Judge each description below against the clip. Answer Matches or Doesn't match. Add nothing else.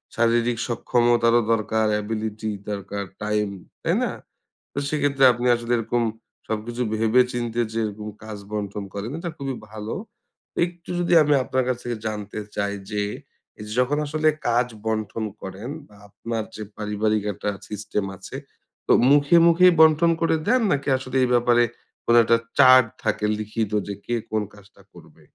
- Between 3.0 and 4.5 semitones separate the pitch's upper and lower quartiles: Matches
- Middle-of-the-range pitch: Doesn't match